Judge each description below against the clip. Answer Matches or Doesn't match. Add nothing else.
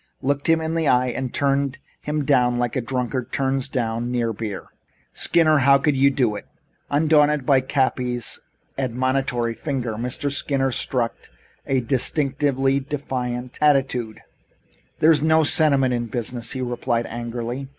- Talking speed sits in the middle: Matches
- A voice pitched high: Doesn't match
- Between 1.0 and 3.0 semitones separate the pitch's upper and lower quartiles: Matches